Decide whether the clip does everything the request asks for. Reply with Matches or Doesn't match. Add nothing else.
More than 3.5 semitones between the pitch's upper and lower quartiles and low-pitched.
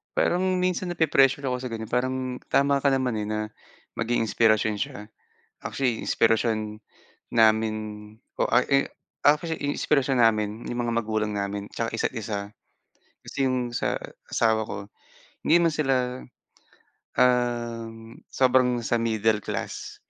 Doesn't match